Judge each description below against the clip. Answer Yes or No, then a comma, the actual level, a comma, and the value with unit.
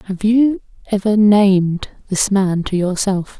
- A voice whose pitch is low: No, high, 200 Hz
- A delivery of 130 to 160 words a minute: Yes, average, 140 wpm